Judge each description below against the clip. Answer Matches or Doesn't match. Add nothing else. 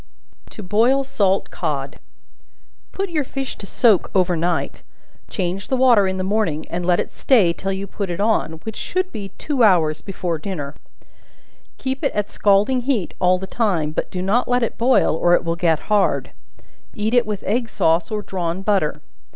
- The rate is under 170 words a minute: Doesn't match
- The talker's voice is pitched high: Matches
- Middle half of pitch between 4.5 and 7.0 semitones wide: Matches